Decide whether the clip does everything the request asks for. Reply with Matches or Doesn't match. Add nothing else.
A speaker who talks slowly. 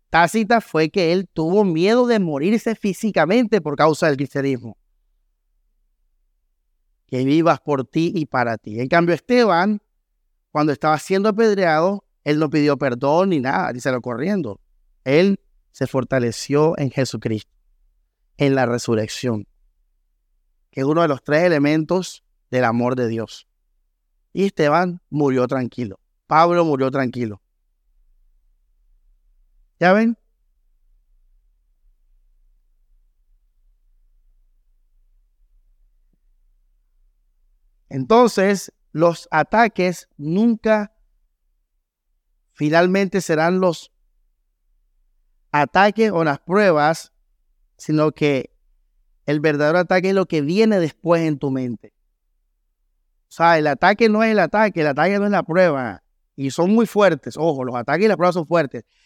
Matches